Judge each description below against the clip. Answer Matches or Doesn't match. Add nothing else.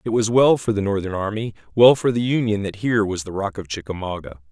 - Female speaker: Doesn't match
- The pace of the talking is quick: Matches